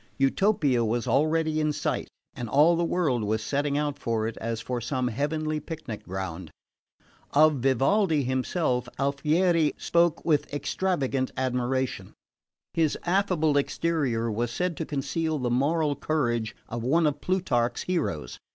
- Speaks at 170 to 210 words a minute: No, average, 140 wpm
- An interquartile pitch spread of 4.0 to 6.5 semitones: Yes, average, 4.8 semitones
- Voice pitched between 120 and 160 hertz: Yes, medium, 140 Hz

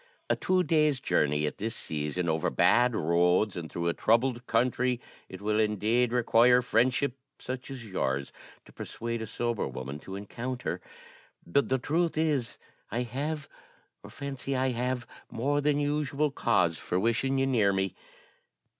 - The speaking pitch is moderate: No, low, 120 Hz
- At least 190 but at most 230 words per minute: No, average, 155 wpm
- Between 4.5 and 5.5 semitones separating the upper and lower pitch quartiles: Yes, average, 5.2 semitones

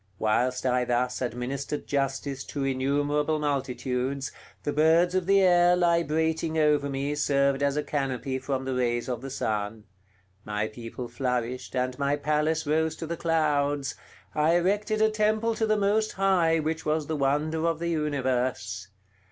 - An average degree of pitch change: Yes, average, 3.9 semitones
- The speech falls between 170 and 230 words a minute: No, average, 160 wpm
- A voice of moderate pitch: Yes, medium, 145 Hz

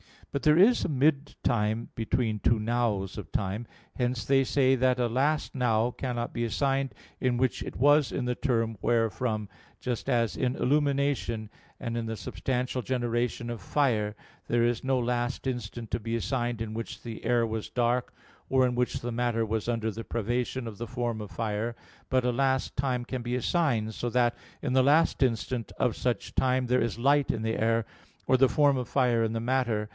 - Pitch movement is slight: Yes, narrow, 2.3 semitones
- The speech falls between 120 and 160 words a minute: No, average, 195 wpm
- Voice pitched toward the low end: Yes, low, 120 Hz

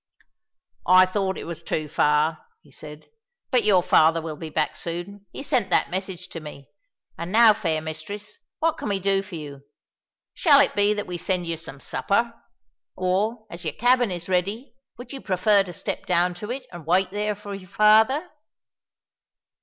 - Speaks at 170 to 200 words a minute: Yes, average, 185 wpm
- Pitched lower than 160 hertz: No, medium, 185 Hz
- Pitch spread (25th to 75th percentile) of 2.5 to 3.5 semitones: No, average, 4.1 semitones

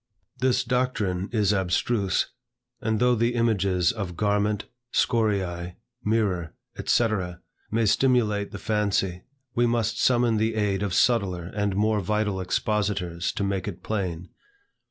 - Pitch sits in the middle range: No, low, 105 Hz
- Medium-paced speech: No, slow, 130 wpm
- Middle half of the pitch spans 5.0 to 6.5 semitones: No, average, 3.1 semitones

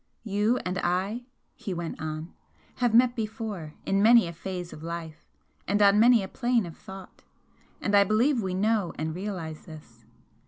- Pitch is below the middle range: No, high, 195 Hz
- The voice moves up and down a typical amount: Yes, average, 4.7 semitones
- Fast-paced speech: No, average, 170 wpm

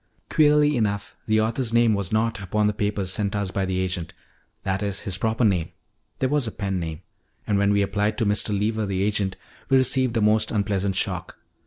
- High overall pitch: No, low, 105 Hz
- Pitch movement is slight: Yes, narrow, 2.3 semitones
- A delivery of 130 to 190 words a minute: No, fast, 205 wpm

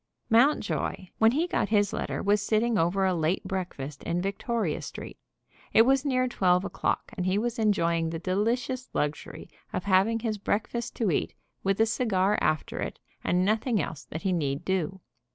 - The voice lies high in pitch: Yes, high, 195 Hz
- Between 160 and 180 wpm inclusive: Yes, average, 175 wpm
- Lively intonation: No, average, 4.1 semitones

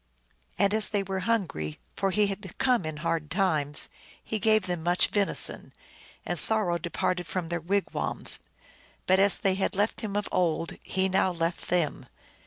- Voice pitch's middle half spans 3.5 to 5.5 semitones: No, average, 3.1 semitones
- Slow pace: No, average, 175 wpm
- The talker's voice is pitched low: No, high, 190 Hz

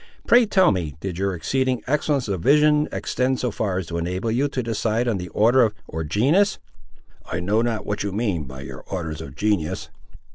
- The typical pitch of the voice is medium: No, low, 105 Hz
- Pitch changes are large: Yes, wide, 6.5 semitones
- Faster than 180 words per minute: Yes, average, 195 wpm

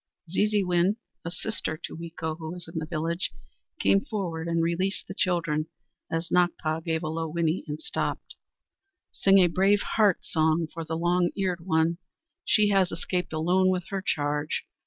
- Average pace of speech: Yes, average, 165 wpm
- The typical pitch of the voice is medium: Yes, medium, 170 Hz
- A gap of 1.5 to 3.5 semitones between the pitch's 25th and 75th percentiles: Yes, narrow, 2.5 semitones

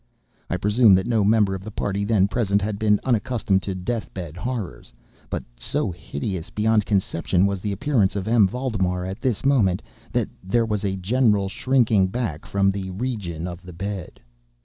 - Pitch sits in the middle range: No, low, 100 Hz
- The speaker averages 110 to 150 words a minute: No, average, 180 wpm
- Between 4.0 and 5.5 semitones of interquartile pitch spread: No, average, 3.1 semitones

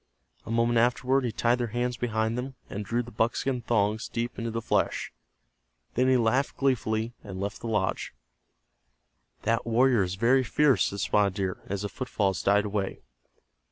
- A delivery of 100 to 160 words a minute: No, average, 170 wpm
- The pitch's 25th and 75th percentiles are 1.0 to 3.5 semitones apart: Yes, average, 3.1 semitones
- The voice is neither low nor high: No, low, 115 Hz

